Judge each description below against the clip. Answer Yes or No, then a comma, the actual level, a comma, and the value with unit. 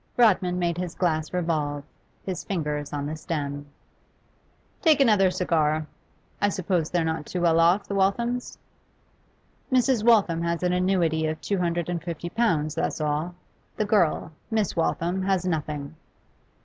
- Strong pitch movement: No, average, 3.5 semitones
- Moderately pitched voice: Yes, medium, 175 Hz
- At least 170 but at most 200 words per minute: No, average, 150 wpm